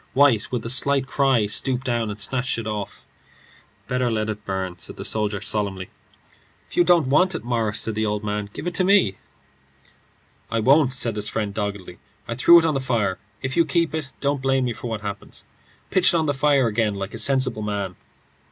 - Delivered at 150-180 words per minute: No, fast, 205 wpm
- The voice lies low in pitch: Yes, low, 115 Hz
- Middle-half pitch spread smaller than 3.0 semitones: No, average, 4.6 semitones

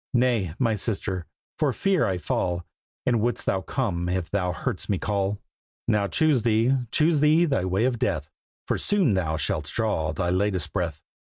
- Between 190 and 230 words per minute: No, average, 175 wpm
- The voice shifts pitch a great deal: Yes, wide, 5.9 semitones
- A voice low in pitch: Yes, low, 100 Hz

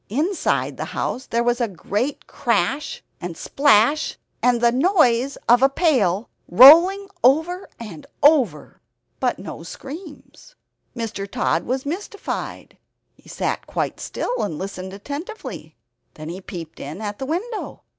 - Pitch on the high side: Yes, very high, 255 Hz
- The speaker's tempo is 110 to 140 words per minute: Yes, slow, 135 wpm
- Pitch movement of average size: No, wide, 7.4 semitones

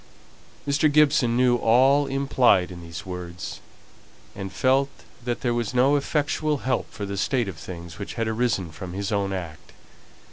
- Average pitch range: No, wide, 6.2 semitones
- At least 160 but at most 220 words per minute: Yes, average, 165 wpm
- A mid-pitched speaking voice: No, low, 115 Hz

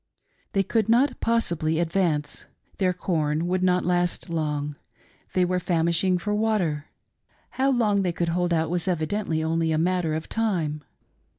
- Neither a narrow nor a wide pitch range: Yes, average, 3.4 semitones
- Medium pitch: Yes, medium, 175 Hz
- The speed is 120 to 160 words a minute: Yes, average, 155 wpm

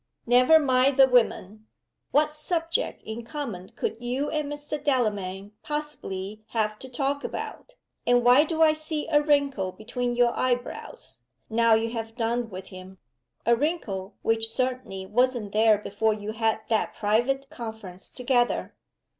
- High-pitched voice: Yes, high, 240 Hz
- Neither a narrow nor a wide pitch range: Yes, average, 4.5 semitones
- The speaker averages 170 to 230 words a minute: No, average, 145 wpm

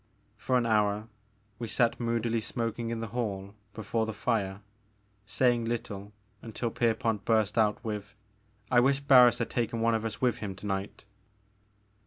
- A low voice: Yes, low, 115 Hz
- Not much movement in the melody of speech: Yes, narrow, 2.1 semitones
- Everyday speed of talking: Yes, average, 160 wpm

